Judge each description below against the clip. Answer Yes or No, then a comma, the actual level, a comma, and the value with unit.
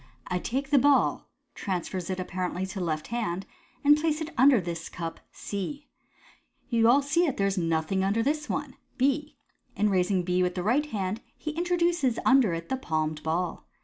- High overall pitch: Yes, high, 205 Hz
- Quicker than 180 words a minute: Yes, average, 190 wpm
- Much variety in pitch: Yes, wide, 7.8 semitones